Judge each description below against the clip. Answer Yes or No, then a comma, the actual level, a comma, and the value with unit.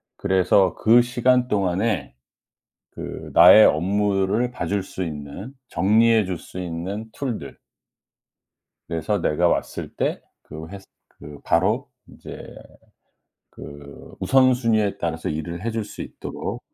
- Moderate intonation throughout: Yes, average, 4.9 semitones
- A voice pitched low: Yes, low, 100 Hz